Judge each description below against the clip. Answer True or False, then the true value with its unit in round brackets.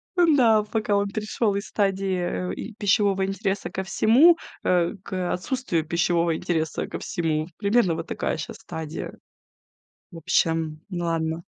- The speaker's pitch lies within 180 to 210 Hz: True (190 Hz)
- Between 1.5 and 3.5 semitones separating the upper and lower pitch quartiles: False (4.0 semitones)